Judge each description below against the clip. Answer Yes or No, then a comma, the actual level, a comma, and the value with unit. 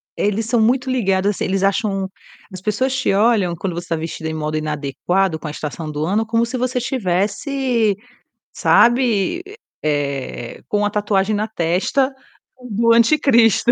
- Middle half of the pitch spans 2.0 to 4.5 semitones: No, average, 5.2 semitones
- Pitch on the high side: Yes, high, 205 Hz